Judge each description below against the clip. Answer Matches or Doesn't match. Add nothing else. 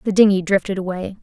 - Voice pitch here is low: Doesn't match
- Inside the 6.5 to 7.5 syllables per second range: Matches